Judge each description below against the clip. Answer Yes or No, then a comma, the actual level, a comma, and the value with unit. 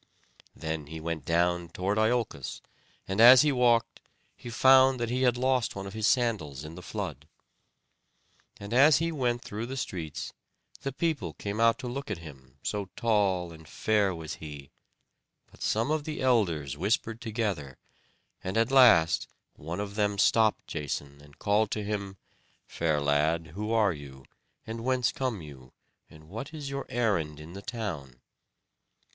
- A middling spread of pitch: No, wide, 7.0 semitones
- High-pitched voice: No, low, 105 Hz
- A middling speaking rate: Yes, average, 165 wpm